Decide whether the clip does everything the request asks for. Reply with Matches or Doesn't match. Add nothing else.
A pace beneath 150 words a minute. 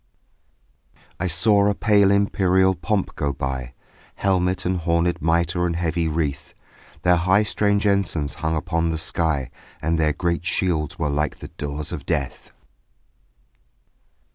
Matches